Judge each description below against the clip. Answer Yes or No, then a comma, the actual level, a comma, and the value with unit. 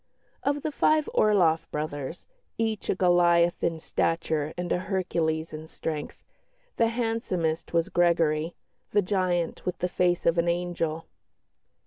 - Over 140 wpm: No, slow, 135 wpm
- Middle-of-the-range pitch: Yes, medium, 175 Hz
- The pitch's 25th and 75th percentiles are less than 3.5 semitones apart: Yes, narrow, 2.5 semitones